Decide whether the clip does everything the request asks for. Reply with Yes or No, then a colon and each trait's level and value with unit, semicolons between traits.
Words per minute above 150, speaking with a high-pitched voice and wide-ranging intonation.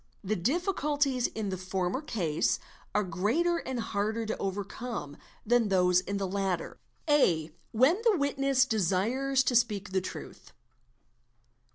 No: slow, 135 wpm; high, 220 Hz; wide, 6.1 semitones